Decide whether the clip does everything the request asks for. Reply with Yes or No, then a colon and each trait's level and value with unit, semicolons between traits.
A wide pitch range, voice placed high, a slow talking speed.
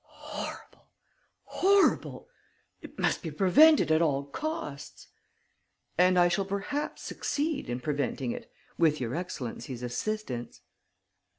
No: wide, 7.5 semitones; medium, 170 Hz; slow, 110 wpm